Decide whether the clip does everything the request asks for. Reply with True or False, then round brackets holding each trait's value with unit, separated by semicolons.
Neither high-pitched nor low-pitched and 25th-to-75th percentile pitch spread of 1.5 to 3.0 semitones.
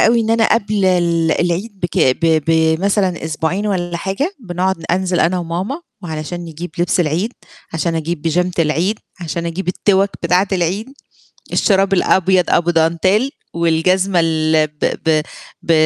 True (175 Hz; 2.7 semitones)